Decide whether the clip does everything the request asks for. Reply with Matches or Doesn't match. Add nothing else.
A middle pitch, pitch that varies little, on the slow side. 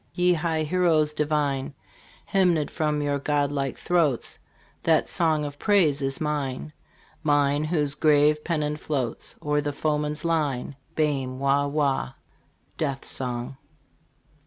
Matches